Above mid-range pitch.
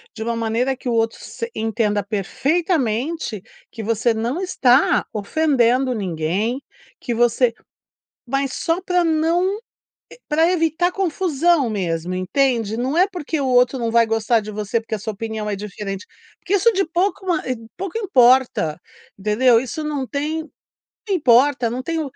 Yes: very high, 250 Hz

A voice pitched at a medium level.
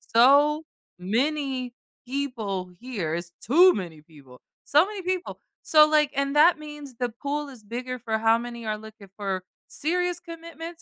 No: very high, 255 Hz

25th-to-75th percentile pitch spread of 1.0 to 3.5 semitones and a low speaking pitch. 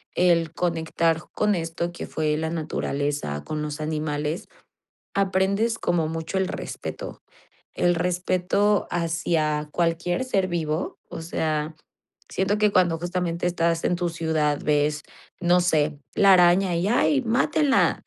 No: average, 2.7 semitones; medium, 170 Hz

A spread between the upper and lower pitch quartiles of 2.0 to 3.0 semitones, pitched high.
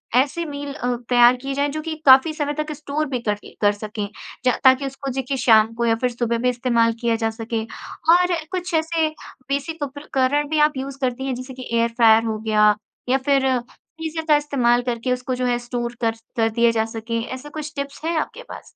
No: average, 3.5 semitones; very high, 260 Hz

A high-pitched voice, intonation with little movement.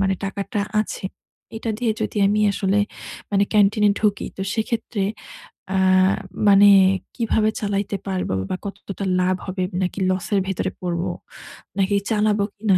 Yes: high, 200 Hz; narrow, 1.7 semitones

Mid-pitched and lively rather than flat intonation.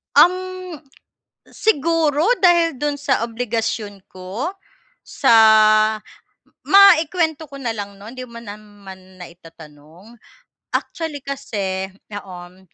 No: high, 225 Hz; wide, 7.7 semitones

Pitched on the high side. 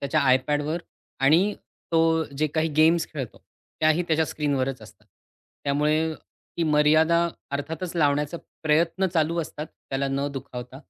No: medium, 155 Hz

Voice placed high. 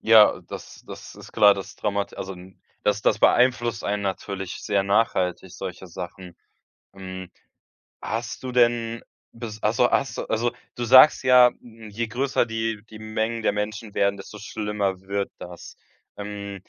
No: low, 105 Hz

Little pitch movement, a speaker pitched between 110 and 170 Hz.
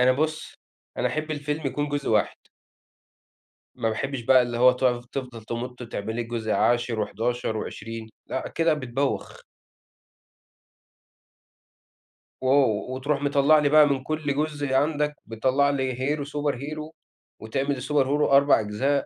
No: average, 3.3 semitones; low, 135 Hz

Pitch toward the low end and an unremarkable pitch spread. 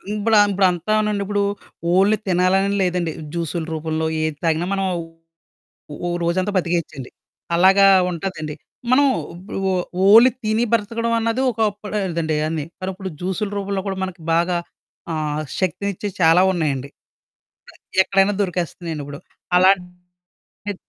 No: medium, 185 Hz; average, 3.2 semitones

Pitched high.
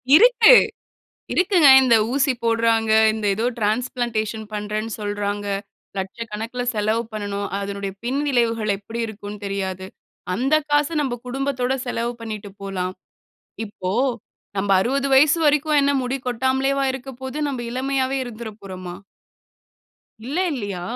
Yes: high, 230 Hz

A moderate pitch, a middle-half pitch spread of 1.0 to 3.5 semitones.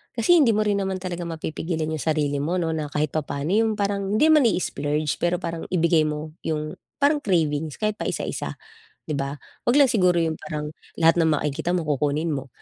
No: medium, 165 Hz; average, 4.3 semitones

